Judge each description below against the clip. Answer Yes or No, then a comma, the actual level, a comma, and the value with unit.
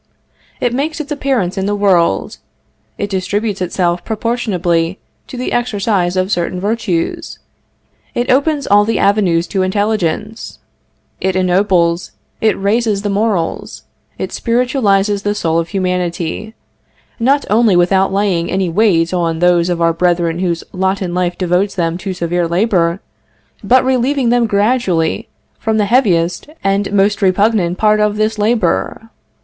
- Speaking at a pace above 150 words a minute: No, average, 145 wpm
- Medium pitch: No, high, 195 Hz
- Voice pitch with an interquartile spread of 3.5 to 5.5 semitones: Yes, average, 3.9 semitones